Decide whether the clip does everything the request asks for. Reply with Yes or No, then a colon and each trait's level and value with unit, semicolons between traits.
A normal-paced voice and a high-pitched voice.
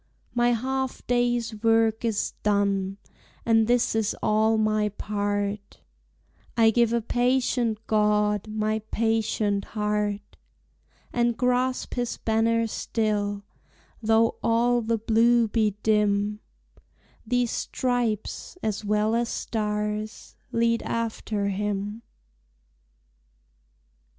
No: slow, 100 wpm; high, 220 Hz